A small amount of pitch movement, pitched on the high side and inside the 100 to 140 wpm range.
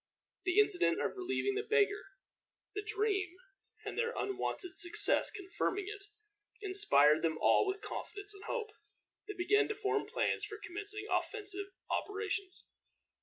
Yes: narrow, 1.7 semitones; very high, 405 Hz; slow, 135 wpm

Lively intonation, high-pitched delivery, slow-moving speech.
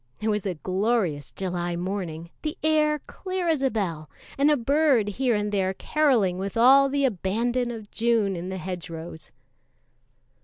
No: wide, 6.5 semitones; high, 210 Hz; average, 160 wpm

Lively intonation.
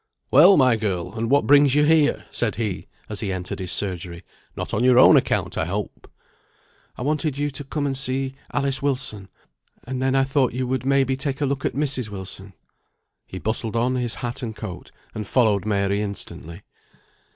No: average, 5.0 semitones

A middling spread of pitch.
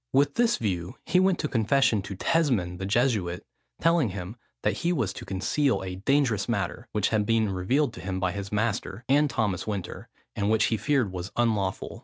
No: wide, 6.0 semitones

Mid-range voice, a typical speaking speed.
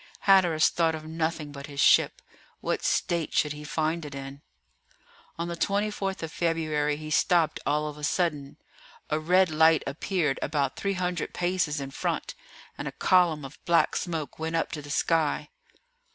Yes: medium, 160 Hz; average, 165 wpm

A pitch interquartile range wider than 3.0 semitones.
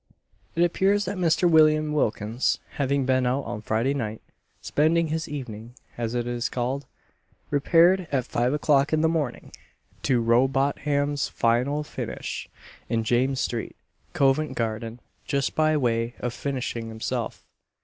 Yes: average, 4.2 semitones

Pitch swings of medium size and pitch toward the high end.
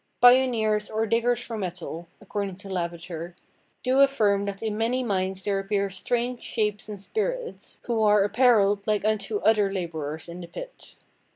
Yes: average, 3.2 semitones; high, 210 Hz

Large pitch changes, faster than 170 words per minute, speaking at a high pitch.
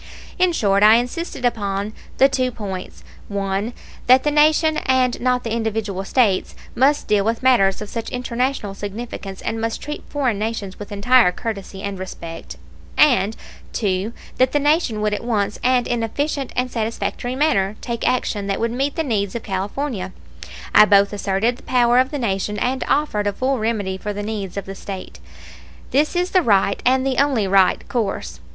No: average, 4.3 semitones; average, 180 wpm; high, 225 Hz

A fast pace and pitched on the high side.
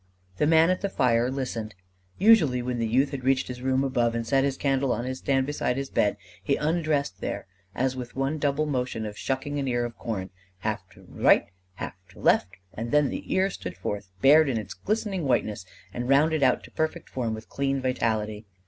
No: fast, 210 wpm; low, 130 Hz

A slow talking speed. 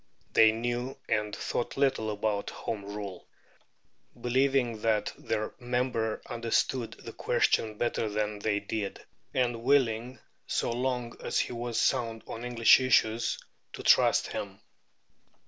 Yes: slow, 130 wpm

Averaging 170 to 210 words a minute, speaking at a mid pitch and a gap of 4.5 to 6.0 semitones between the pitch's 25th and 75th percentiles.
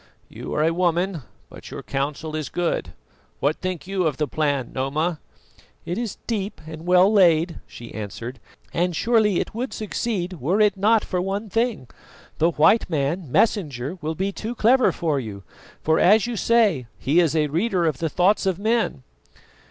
Yes: average, 175 wpm; medium, 175 Hz; average, 5.1 semitones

